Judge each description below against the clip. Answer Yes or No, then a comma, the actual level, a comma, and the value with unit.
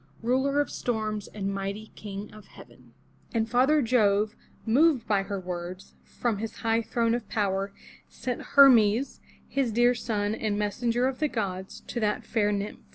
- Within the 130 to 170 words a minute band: Yes, average, 160 wpm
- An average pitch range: Yes, average, 3.1 semitones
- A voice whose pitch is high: Yes, high, 220 Hz